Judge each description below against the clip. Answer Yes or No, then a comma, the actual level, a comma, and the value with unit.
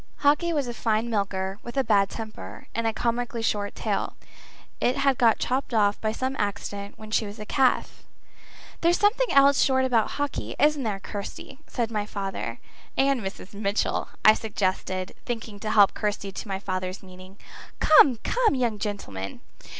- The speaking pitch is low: No, high, 220 Hz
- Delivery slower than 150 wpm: No, average, 170 wpm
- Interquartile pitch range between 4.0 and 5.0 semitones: Yes, average, 4.5 semitones